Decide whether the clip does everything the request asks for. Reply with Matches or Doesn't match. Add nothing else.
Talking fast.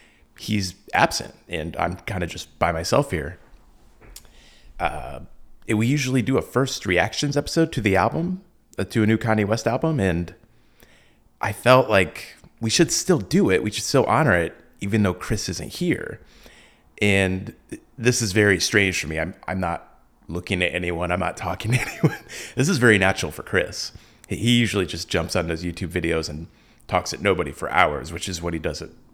Doesn't match